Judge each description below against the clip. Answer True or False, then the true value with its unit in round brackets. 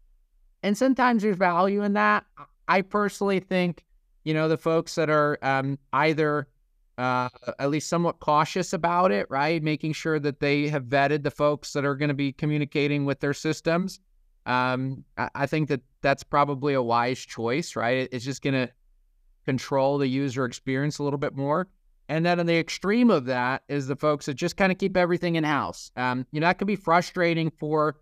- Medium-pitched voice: True (150 Hz)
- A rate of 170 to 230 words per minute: True (195 wpm)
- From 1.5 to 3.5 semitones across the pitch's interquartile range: False (3.9 semitones)